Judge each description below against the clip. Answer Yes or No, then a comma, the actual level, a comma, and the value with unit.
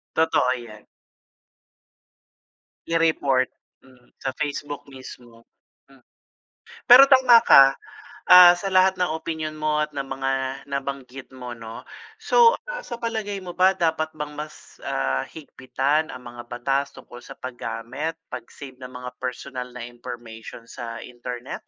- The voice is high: No, low, 135 Hz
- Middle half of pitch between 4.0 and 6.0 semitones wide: Yes, average, 4.6 semitones